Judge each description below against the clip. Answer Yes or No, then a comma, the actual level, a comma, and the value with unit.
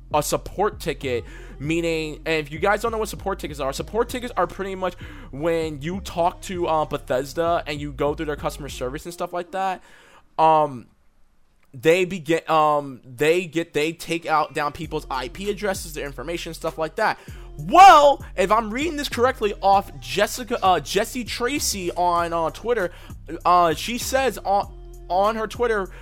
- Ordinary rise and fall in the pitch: Yes, average, 4.6 semitones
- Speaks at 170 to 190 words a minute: Yes, average, 175 wpm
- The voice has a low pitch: No, medium, 170 Hz